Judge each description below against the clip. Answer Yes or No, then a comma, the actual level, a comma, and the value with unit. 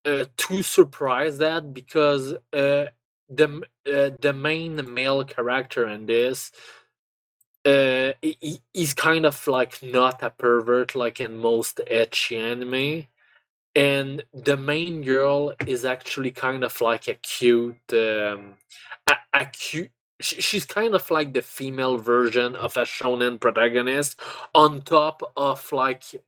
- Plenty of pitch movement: No, average, 3.5 semitones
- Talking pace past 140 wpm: No, slow, 135 wpm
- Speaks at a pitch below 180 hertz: Yes, low, 135 Hz